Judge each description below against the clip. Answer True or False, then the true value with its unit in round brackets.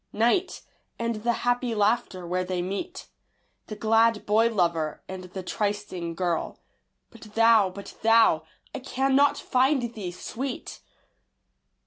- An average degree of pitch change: True (4.5 semitones)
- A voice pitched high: True (215 Hz)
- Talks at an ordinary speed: False (125 wpm)